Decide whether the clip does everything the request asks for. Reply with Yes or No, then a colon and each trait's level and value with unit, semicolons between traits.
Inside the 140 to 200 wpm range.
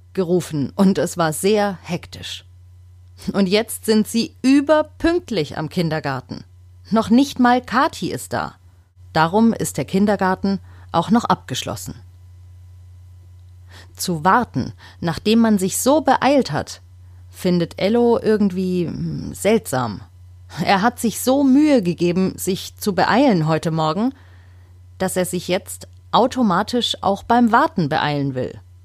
No: slow, 125 wpm